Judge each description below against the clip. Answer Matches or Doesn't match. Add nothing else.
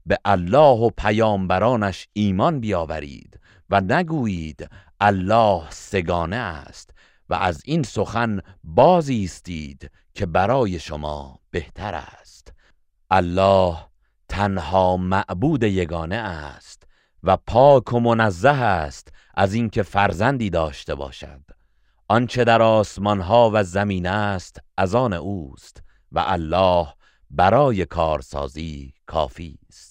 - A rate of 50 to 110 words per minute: Matches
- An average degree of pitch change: Matches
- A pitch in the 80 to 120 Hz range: Matches